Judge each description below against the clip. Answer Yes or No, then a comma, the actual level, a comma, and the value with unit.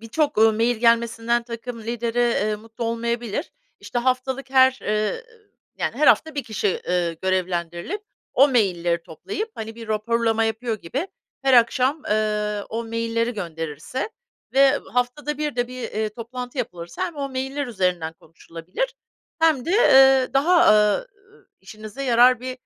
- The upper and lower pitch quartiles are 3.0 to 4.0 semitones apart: Yes, average, 3.7 semitones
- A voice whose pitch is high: Yes, high, 235 Hz